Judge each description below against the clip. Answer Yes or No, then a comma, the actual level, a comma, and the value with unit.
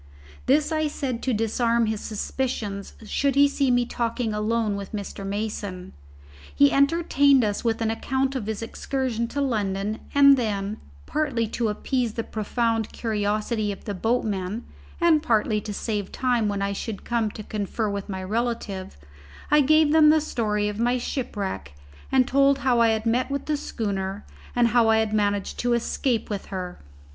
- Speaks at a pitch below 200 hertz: No, high, 225 Hz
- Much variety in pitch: No, average, 3.8 semitones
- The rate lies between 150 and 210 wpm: Yes, average, 170 wpm